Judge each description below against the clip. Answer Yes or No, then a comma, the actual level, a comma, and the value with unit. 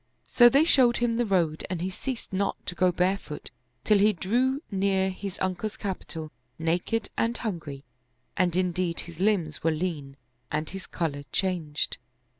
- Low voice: No, medium, 185 Hz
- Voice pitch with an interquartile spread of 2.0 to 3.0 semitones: No, average, 4.1 semitones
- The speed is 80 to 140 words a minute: No, average, 160 wpm